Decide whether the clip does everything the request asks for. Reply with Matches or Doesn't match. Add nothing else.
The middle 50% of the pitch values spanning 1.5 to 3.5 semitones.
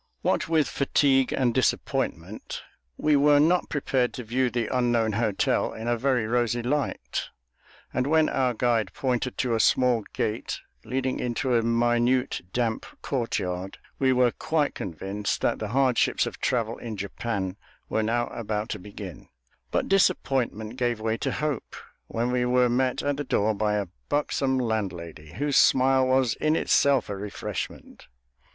Matches